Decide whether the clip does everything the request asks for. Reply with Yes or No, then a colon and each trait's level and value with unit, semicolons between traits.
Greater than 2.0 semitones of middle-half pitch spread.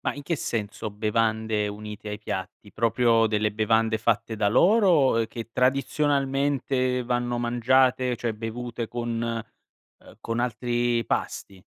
Yes: narrow, 2.4 semitones